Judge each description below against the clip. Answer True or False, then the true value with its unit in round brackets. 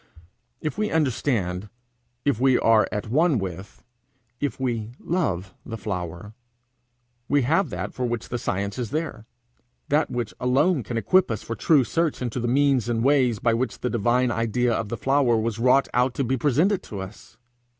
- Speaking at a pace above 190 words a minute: False (180 wpm)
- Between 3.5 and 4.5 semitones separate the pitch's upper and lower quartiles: True (4.1 semitones)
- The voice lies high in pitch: False (125 Hz)